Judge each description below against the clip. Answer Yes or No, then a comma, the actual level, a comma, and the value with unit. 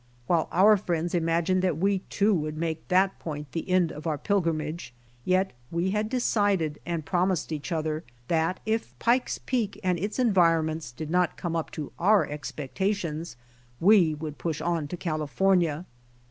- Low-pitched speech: No, medium, 170 Hz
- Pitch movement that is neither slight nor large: Yes, average, 3.4 semitones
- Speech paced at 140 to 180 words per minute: Yes, average, 160 wpm